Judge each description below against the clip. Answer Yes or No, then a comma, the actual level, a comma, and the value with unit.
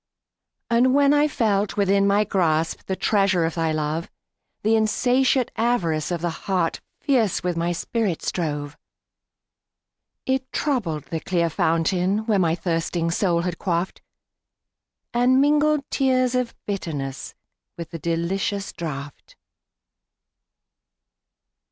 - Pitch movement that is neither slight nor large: No, wide, 6.0 semitones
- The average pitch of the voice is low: No, high, 190 Hz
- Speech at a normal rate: No, slow, 110 wpm